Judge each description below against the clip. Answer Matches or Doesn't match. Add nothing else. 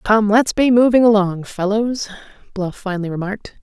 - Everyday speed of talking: Matches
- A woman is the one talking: Matches